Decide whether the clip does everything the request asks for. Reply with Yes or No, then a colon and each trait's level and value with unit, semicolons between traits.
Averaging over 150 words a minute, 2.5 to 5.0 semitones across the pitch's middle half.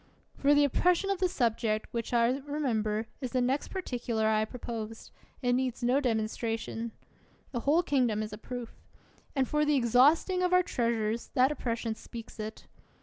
Yes: average, 170 wpm; average, 4.1 semitones